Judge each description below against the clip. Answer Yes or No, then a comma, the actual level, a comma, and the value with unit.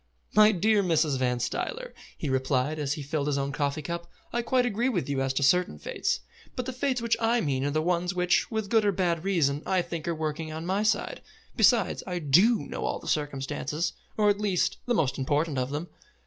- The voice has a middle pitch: Yes, medium, 170 Hz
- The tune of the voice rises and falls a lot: Yes, wide, 6.3 semitones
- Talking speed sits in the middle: No, fast, 220 wpm